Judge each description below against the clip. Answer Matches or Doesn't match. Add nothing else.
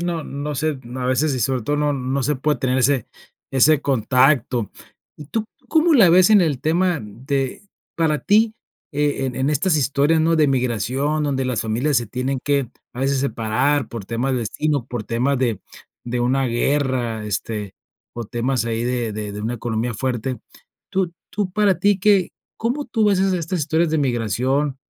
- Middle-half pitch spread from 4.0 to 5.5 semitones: Matches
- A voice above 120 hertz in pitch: Matches